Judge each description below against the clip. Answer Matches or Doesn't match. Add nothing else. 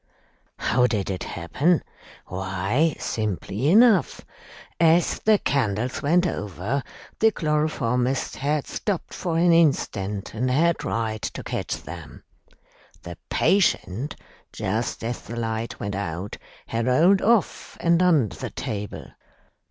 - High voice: Doesn't match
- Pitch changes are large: Matches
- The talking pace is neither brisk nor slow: Doesn't match